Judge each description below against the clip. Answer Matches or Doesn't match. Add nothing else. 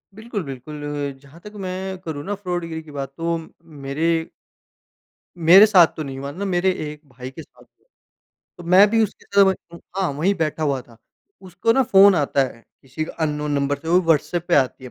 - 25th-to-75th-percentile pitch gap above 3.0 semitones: Matches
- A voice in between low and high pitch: Matches